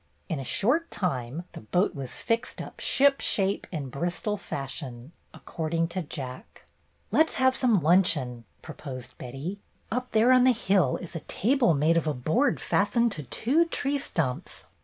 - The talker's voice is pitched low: No, medium, 175 Hz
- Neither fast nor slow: Yes, average, 165 wpm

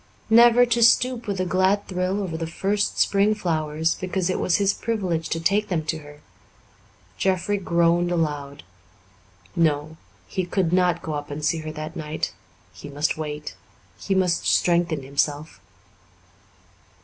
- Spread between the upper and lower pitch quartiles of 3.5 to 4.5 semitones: Yes, average, 3.8 semitones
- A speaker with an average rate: Yes, average, 150 wpm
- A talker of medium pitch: Yes, medium, 170 Hz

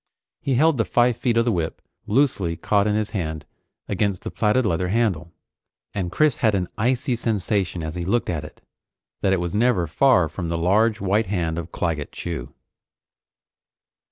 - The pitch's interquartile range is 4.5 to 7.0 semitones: Yes, average, 5.2 semitones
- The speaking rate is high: No, average, 180 wpm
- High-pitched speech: No, low, 100 Hz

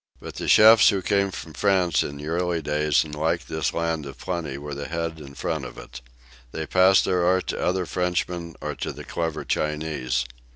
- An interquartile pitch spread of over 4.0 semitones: No, average, 3.1 semitones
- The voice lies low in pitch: Yes, very low, 80 Hz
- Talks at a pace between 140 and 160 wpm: No, fast, 205 wpm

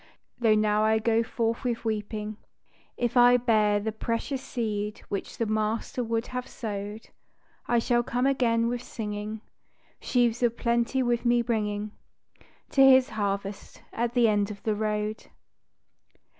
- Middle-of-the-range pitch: No, high, 225 Hz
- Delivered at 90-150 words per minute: Yes, average, 145 wpm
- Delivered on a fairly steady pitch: Yes, narrow, 2.2 semitones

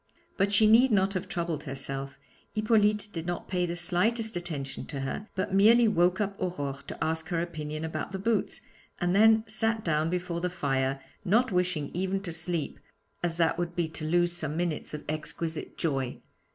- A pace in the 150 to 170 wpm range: No, average, 185 wpm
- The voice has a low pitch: No, medium, 175 Hz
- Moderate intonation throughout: Yes, average, 4.0 semitones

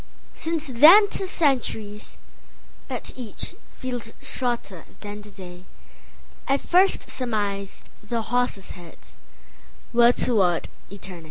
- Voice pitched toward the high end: Yes, high, 230 Hz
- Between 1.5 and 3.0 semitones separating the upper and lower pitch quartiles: No, average, 4.5 semitones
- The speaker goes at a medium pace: No, slow, 90 wpm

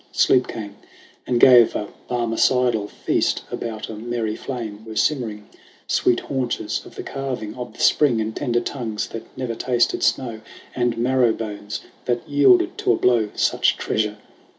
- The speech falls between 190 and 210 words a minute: No, average, 155 wpm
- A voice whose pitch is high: No, low, 120 Hz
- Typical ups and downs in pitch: No, narrow, 2.3 semitones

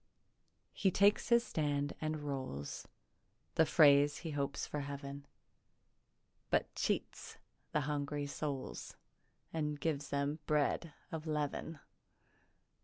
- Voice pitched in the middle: Yes, medium, 145 Hz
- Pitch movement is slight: Yes, narrow, 1.6 semitones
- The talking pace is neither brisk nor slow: No, slow, 110 wpm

